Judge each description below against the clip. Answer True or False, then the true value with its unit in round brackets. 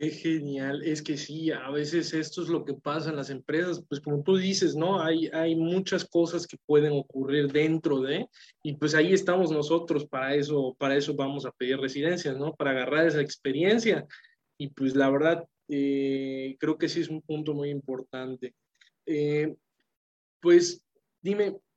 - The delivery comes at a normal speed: True (175 wpm)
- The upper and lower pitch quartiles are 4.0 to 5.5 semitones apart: False (2.8 semitones)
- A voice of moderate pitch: True (150 Hz)